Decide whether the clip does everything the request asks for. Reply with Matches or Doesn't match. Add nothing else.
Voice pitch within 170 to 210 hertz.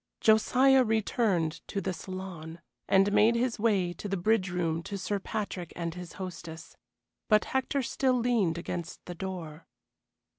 Matches